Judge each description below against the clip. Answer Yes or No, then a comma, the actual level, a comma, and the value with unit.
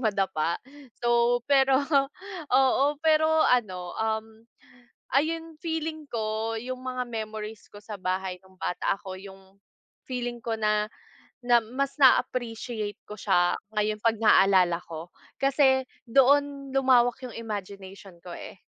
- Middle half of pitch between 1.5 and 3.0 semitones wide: No, average, 4.8 semitones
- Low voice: No, high, 225 Hz